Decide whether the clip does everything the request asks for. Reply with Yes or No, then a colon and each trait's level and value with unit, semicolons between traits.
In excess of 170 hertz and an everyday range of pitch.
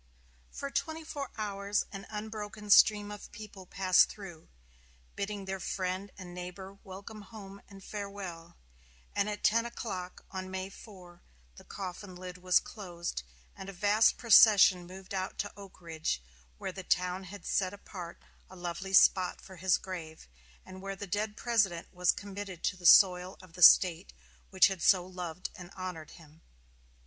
No: high, 190 Hz; narrow, 2.2 semitones